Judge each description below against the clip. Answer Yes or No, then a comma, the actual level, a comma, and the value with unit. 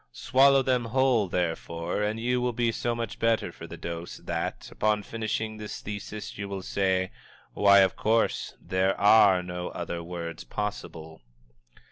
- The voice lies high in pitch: No, low, 105 Hz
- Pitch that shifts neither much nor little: Yes, average, 4.1 semitones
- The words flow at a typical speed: Yes, average, 155 wpm